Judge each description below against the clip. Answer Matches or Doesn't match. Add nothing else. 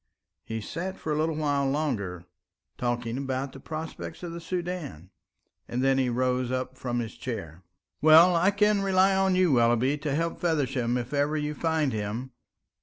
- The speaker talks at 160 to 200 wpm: Matches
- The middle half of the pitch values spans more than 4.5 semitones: Matches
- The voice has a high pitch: Doesn't match